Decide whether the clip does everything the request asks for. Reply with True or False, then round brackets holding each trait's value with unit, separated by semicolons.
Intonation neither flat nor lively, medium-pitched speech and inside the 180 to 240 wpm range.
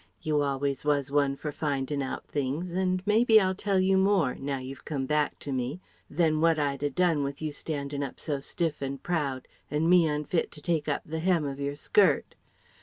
True (3.5 semitones; 150 Hz; 205 wpm)